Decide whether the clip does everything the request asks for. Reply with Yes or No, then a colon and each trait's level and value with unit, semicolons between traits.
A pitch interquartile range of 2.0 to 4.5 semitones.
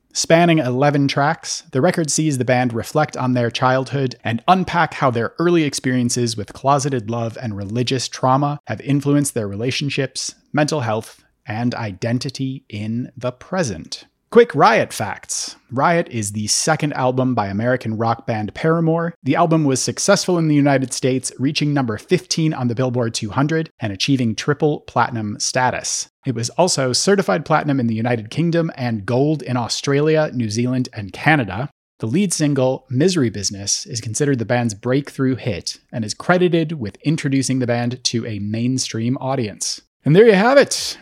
Yes: average, 4.0 semitones